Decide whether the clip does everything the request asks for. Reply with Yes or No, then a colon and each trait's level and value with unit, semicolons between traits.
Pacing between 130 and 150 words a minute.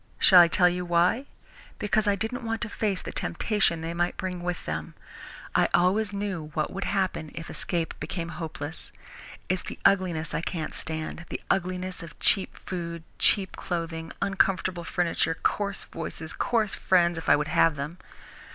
No: average, 170 wpm